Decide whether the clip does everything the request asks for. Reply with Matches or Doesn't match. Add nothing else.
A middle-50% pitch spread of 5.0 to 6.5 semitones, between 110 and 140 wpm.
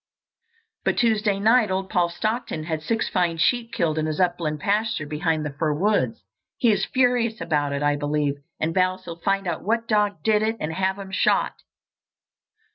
Doesn't match